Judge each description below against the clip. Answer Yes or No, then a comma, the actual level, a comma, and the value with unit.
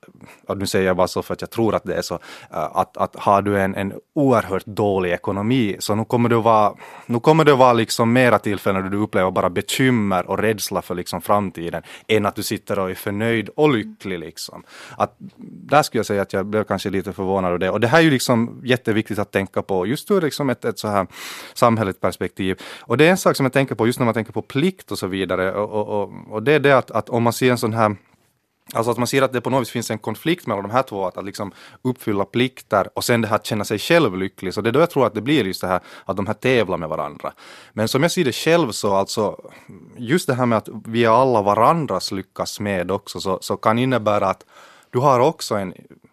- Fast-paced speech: Yes, fast, 250 wpm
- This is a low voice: Yes, low, 110 Hz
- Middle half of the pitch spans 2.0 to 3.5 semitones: No, average, 4.1 semitones